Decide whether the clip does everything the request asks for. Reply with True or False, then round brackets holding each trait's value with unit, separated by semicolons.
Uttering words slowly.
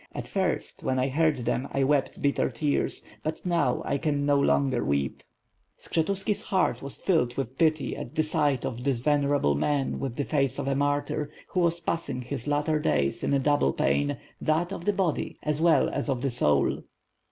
False (190 wpm)